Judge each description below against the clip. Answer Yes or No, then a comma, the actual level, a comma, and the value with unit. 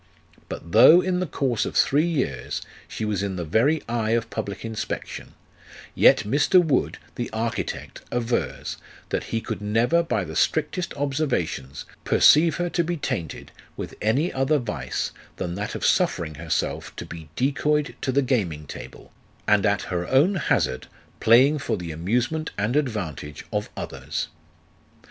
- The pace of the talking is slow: No, average, 155 wpm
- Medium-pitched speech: No, low, 115 Hz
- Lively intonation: Yes, wide, 7.1 semitones